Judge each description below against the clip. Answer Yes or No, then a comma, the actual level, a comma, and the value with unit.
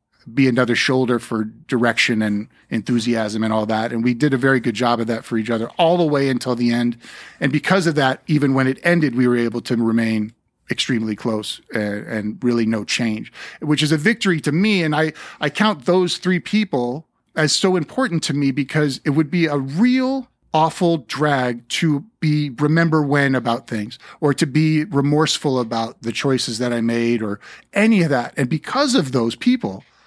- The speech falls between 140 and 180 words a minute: No, average, 200 wpm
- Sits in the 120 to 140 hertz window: Yes, low, 135 Hz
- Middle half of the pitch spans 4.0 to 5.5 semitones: Yes, average, 5.1 semitones